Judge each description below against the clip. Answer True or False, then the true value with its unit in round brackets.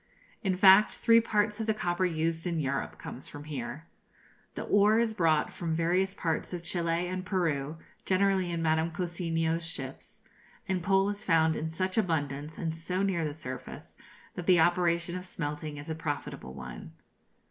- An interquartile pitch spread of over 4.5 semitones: False (2.8 semitones)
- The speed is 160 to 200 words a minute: True (170 wpm)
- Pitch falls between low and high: True (170 Hz)